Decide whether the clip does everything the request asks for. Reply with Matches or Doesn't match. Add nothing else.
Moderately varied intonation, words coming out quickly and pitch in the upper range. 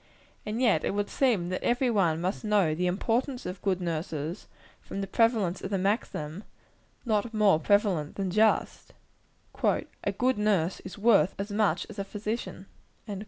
Doesn't match